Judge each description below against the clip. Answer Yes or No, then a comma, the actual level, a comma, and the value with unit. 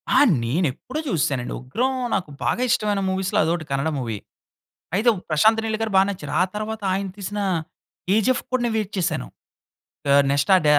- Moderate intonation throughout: No, wide, 6.7 semitones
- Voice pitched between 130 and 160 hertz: No, high, 195 Hz